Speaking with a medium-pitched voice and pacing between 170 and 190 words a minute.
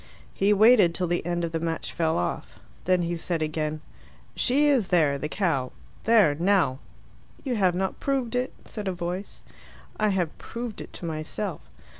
Yes: medium, 180 Hz; average, 175 wpm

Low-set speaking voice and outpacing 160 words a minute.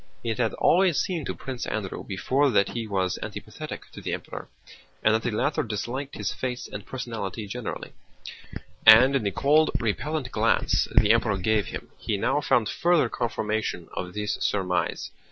Yes: low, 115 Hz; average, 170 wpm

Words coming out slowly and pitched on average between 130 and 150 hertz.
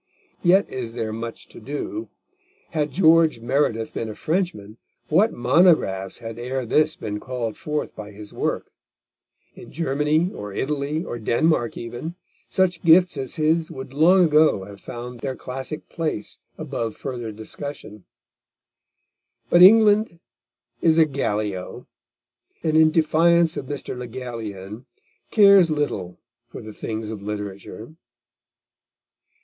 Yes: slow, 130 wpm; low, 135 Hz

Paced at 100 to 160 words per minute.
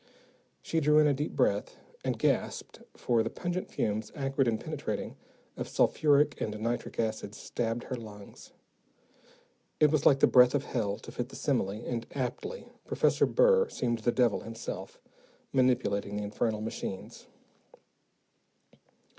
Yes: average, 145 wpm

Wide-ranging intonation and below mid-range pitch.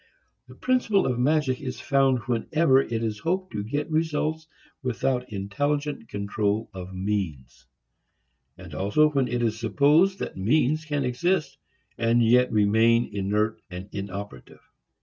Yes: wide, 6.3 semitones; low, 120 Hz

